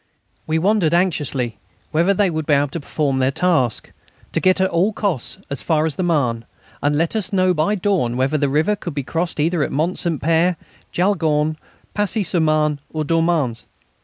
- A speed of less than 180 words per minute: No, average, 190 wpm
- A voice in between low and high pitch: Yes, medium, 160 Hz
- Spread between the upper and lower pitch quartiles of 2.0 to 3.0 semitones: No, average, 3.8 semitones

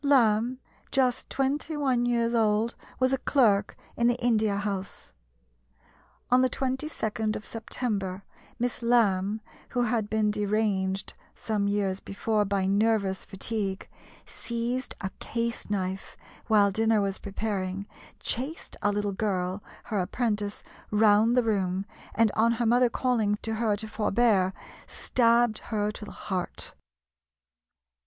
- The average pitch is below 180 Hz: No, high, 215 Hz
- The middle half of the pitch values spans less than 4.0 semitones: Yes, average, 2.9 semitones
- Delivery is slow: Yes, slow, 130 wpm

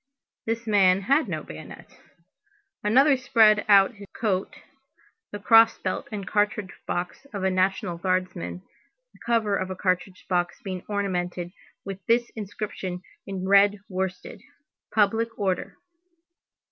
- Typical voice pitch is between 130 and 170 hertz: No, high, 195 Hz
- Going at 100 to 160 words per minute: Yes, slow, 135 wpm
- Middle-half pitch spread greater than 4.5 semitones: No, narrow, 2.5 semitones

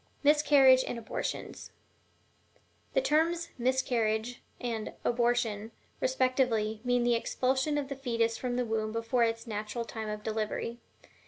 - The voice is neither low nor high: No, high, 240 Hz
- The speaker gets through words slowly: Yes, slow, 130 wpm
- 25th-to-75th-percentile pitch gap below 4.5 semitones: Yes, average, 2.7 semitones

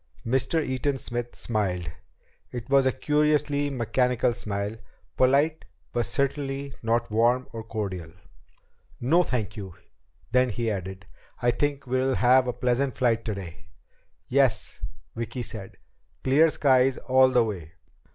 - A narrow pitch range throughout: No, average, 3.4 semitones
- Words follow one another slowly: Yes, slow, 130 wpm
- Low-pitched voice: Yes, low, 125 Hz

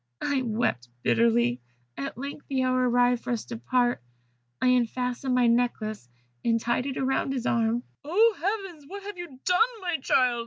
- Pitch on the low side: No, very high, 250 Hz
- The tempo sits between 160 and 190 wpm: Yes, average, 180 wpm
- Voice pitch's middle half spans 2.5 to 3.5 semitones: Yes, average, 3.2 semitones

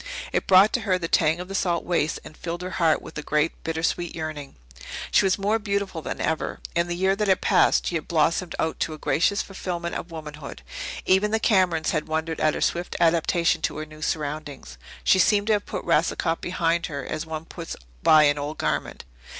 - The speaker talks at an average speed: No, fast, 215 wpm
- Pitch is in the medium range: Yes, medium, 165 Hz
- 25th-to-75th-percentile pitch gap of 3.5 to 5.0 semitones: No, average, 3.0 semitones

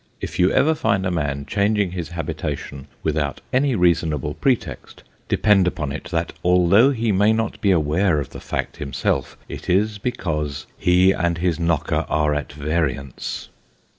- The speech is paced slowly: No, average, 160 wpm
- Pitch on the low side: Yes, very low, 85 Hz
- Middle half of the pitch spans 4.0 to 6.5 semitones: Yes, average, 4.9 semitones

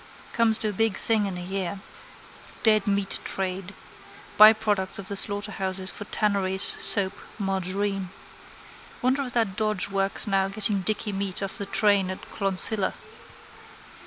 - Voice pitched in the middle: No, high, 200 Hz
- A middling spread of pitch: No, narrow, 1.8 semitones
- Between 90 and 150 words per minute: Yes, average, 140 wpm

